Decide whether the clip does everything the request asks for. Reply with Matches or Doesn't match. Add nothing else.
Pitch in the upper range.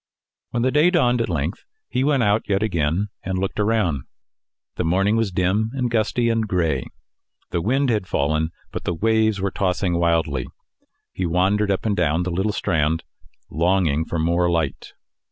Doesn't match